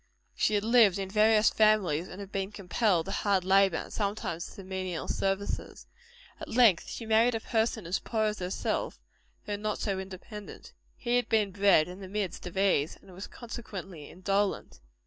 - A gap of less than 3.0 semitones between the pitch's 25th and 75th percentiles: Yes, narrow, 2.4 semitones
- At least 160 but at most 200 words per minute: Yes, average, 180 wpm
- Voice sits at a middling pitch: No, high, 200 Hz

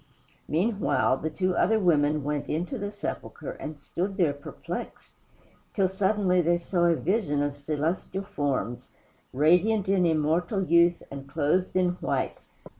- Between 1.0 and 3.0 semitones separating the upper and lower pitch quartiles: No, average, 4.2 semitones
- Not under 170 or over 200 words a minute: No, average, 140 wpm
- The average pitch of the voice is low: No, medium, 170 Hz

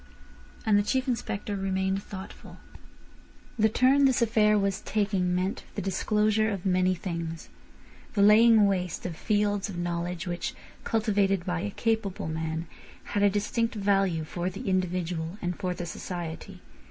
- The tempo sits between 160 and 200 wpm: No, average, 145 wpm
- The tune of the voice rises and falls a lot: No, average, 2.9 semitones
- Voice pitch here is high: Yes, high, 195 Hz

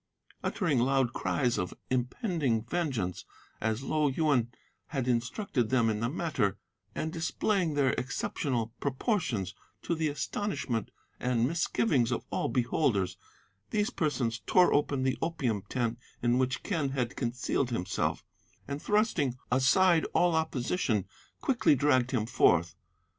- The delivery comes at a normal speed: No, slow, 130 wpm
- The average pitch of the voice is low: Yes, low, 130 Hz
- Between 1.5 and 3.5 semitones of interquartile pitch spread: No, average, 5.1 semitones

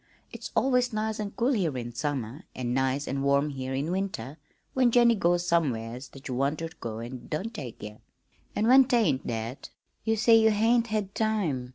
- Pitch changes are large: Yes, wide, 9.0 semitones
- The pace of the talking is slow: No, average, 200 wpm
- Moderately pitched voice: Yes, medium, 155 Hz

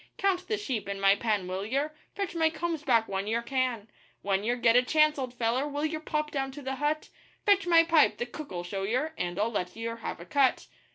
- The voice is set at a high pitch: Yes, very high, 255 Hz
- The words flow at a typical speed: No, fast, 235 wpm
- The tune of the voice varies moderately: No, wide, 6.2 semitones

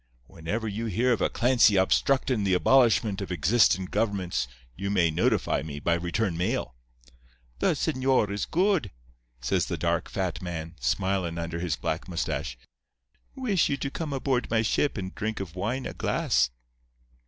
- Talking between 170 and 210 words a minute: No, average, 160 wpm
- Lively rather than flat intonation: Yes, wide, 5.9 semitones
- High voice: No, low, 100 Hz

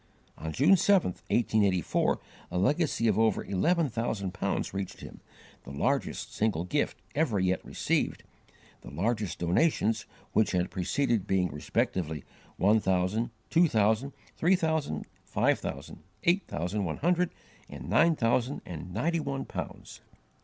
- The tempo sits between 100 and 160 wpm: Yes, average, 140 wpm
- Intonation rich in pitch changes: Yes, wide, 7.8 semitones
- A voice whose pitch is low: Yes, low, 110 Hz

